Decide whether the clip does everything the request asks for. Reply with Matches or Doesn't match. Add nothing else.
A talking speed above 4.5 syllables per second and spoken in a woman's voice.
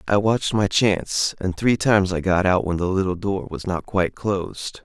Doesn't match